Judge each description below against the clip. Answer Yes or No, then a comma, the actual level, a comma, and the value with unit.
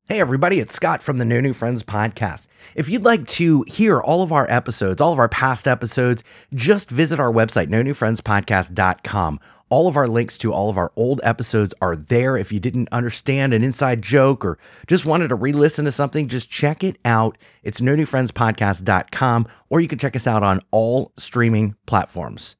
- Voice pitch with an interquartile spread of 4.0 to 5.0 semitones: Yes, average, 4.3 semitones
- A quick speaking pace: No, average, 195 wpm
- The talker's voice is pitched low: Yes, low, 120 Hz